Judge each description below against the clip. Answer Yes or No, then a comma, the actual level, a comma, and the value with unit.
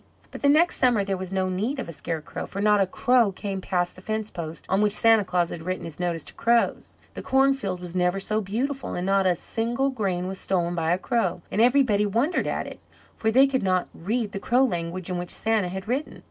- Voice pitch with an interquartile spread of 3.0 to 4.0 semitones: No, average, 4.6 semitones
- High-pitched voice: Yes, high, 195 Hz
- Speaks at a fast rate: Yes, fast, 235 wpm